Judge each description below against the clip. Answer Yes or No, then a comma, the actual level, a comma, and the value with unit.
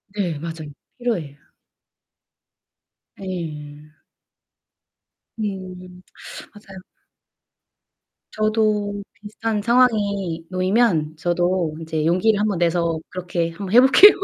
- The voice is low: No, medium, 185 Hz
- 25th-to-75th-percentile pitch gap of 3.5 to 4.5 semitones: Yes, average, 4.1 semitones